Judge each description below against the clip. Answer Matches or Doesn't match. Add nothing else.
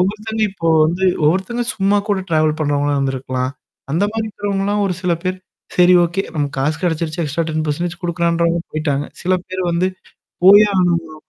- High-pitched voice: Doesn't match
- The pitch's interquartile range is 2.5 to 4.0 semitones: Matches